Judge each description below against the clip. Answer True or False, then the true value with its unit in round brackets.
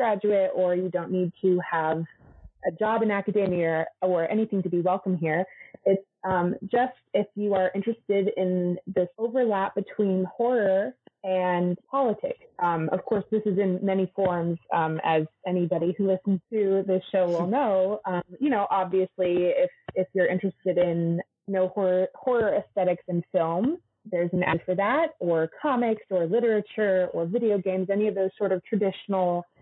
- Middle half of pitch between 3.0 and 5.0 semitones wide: False (2.5 semitones)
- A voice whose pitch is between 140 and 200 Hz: True (190 Hz)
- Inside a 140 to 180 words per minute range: True (170 wpm)